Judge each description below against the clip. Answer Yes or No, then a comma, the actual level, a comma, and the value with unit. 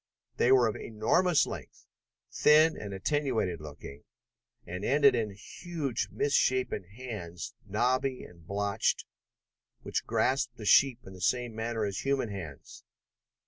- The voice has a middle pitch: No, low, 115 Hz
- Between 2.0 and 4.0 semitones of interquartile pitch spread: No, average, 5.1 semitones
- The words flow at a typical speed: No, slow, 130 wpm